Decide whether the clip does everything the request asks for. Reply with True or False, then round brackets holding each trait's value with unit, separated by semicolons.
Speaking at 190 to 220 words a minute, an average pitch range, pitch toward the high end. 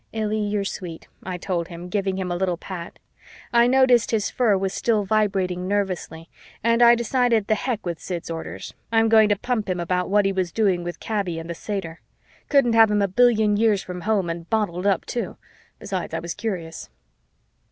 True (195 wpm; 3.6 semitones; 200 Hz)